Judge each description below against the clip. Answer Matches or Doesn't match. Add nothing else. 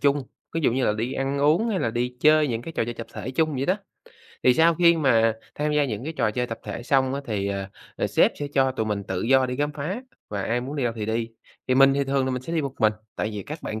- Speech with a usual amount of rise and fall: Matches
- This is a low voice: Matches